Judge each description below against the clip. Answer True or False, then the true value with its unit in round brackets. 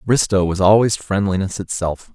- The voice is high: False (95 Hz)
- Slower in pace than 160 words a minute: True (140 wpm)